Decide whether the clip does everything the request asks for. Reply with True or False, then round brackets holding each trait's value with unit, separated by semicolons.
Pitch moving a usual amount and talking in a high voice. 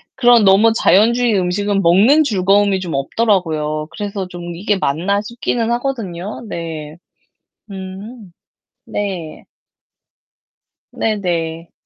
True (4.0 semitones; 195 Hz)